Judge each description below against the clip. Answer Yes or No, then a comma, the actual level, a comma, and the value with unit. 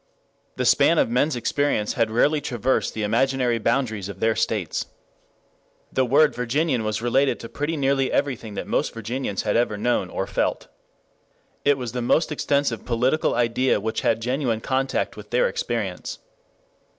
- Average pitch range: Yes, average, 3.4 semitones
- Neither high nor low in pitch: No, low, 125 Hz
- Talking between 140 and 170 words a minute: Yes, average, 160 wpm